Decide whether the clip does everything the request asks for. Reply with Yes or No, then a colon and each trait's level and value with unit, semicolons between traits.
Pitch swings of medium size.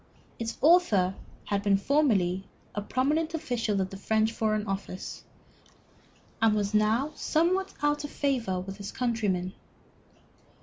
No: wide, 6.4 semitones